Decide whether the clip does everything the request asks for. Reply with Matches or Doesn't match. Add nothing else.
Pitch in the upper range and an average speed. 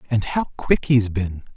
Doesn't match